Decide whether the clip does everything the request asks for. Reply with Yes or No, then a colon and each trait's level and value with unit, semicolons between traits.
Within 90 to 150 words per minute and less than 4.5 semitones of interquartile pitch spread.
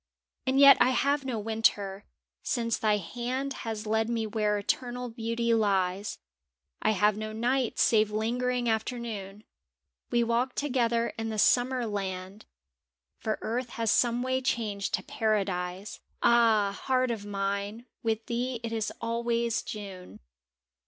Yes: average, 140 wpm; narrow, 2.5 semitones